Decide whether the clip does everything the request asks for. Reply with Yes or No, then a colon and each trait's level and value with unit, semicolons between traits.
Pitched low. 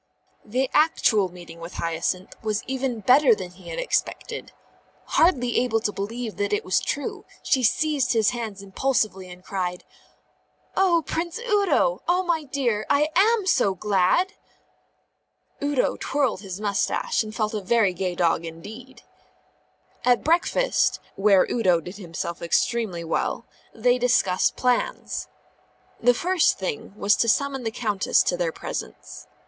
No: high, 230 Hz